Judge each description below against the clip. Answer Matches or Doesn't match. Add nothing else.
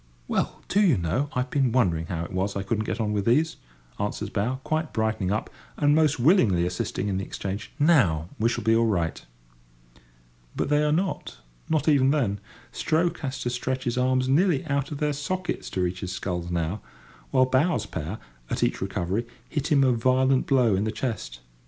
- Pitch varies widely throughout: Matches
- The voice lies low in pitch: Matches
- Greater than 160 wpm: Matches